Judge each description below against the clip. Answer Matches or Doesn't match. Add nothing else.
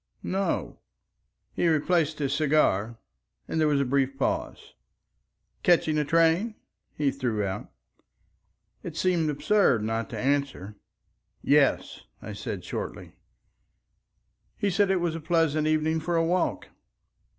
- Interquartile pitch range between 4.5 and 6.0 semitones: Doesn't match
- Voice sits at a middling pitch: Matches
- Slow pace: Matches